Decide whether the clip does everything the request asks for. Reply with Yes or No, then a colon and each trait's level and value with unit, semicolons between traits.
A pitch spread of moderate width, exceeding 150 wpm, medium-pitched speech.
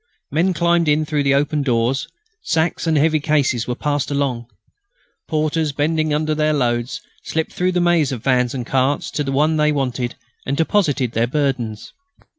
Yes: average, 3.3 semitones; average, 175 wpm; medium, 145 Hz